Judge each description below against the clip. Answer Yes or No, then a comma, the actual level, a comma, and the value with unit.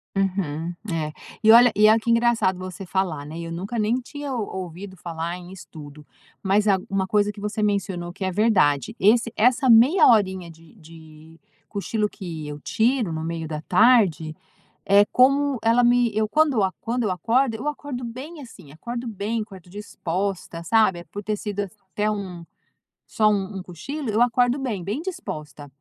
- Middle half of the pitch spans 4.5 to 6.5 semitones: Yes, average, 5.1 semitones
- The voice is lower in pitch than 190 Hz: No, high, 205 Hz